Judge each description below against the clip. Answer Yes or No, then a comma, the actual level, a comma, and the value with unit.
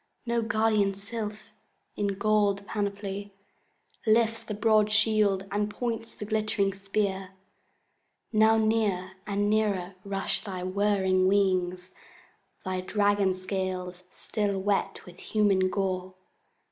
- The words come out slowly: Yes, slow, 110 wpm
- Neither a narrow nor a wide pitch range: No, narrow, 2.1 semitones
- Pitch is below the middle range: No, high, 200 Hz